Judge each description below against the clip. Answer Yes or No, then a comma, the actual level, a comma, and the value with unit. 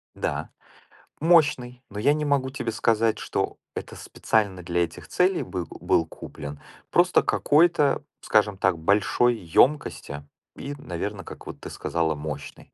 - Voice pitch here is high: No, low, 105 Hz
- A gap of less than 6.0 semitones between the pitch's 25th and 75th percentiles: No, wide, 8.4 semitones